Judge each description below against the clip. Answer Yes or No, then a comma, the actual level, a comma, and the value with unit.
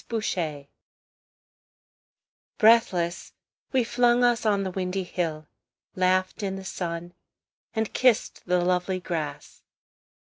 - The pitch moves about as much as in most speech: Yes, average, 4.0 semitones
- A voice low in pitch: No, medium, 185 Hz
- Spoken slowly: Yes, slow, 110 wpm